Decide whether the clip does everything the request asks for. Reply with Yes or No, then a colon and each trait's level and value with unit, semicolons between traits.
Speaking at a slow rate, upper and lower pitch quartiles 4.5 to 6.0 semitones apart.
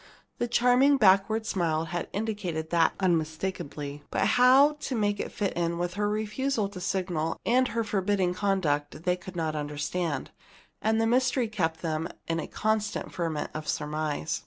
No: average, 160 wpm; average, 5.2 semitones